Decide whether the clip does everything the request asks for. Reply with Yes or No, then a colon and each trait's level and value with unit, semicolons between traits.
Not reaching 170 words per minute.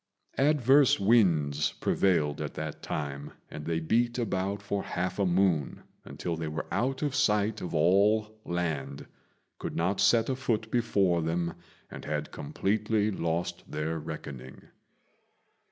Yes: slow, 135 wpm